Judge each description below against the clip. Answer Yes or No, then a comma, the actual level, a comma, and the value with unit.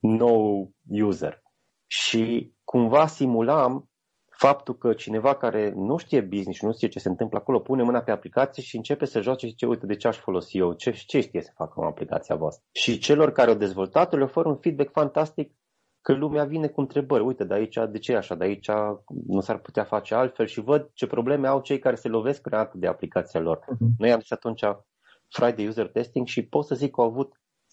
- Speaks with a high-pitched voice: No, low, 120 Hz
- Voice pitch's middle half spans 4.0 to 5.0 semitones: Yes, average, 4.4 semitones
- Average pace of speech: No, fast, 210 wpm